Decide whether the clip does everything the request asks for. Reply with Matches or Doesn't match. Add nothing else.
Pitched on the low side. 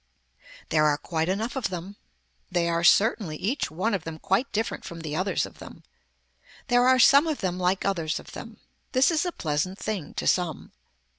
Doesn't match